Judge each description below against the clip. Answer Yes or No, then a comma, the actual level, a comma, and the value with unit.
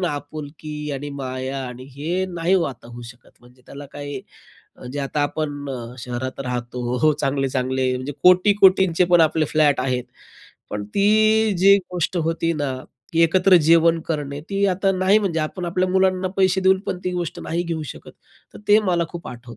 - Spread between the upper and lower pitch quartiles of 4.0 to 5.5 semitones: Yes, average, 5.1 semitones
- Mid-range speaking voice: Yes, medium, 155 Hz